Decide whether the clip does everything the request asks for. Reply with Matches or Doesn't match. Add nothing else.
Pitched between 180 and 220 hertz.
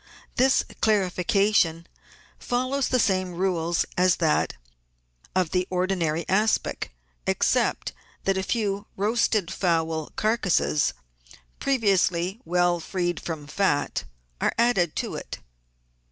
Matches